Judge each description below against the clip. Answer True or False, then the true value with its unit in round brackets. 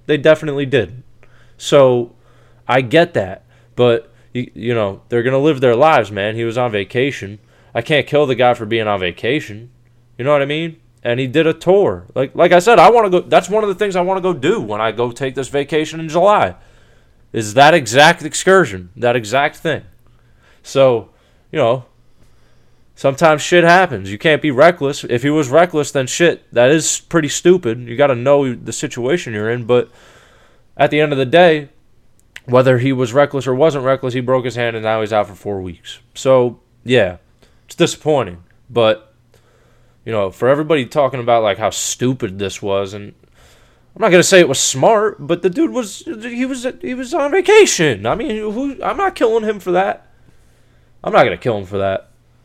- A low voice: True (130 Hz)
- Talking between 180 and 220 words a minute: True (200 wpm)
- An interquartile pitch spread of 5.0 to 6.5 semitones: True (5.6 semitones)